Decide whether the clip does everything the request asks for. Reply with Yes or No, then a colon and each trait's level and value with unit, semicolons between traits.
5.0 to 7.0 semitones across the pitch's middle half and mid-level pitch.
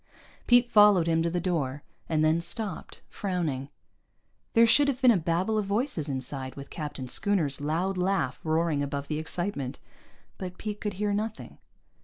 Yes: wide, 5.5 semitones; medium, 170 Hz